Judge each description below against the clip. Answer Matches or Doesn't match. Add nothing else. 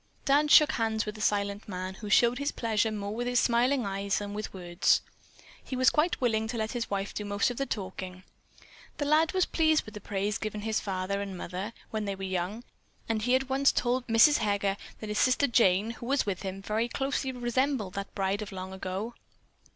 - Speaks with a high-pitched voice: Matches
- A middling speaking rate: Doesn't match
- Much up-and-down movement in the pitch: Doesn't match